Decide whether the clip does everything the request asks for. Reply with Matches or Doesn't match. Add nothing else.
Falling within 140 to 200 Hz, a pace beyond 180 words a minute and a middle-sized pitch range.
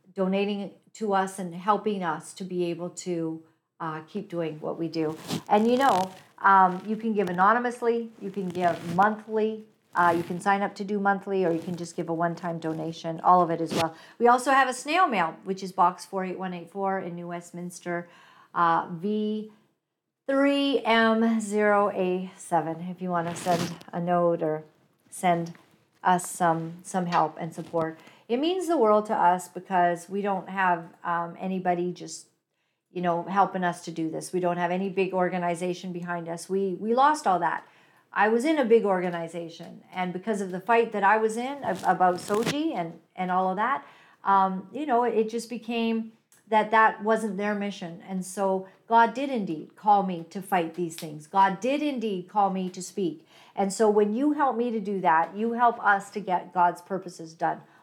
Matches